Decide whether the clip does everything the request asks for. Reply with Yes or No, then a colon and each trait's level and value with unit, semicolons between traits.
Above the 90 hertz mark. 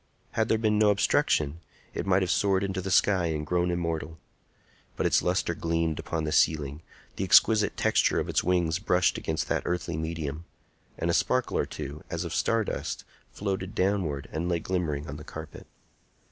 No: very low, 85 Hz